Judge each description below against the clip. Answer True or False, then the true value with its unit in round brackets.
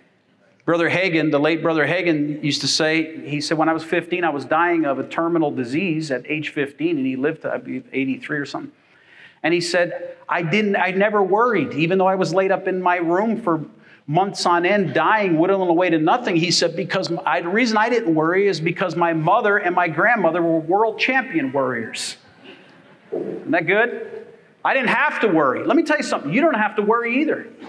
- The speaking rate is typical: False (210 wpm)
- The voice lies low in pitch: False (175 Hz)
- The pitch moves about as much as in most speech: True (4.0 semitones)